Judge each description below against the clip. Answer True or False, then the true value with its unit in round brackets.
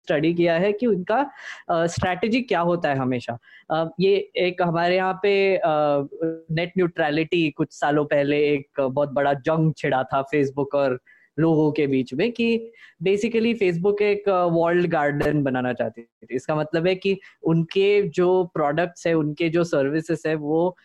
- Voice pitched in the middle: True (165 Hz)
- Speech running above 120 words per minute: True (165 wpm)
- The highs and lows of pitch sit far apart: False (4.0 semitones)